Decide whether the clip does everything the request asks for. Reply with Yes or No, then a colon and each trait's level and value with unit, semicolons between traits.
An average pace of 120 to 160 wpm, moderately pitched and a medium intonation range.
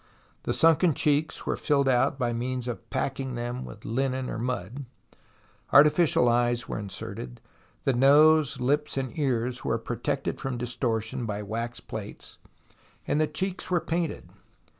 No: average, 150 wpm; low, 130 Hz; average, 3.5 semitones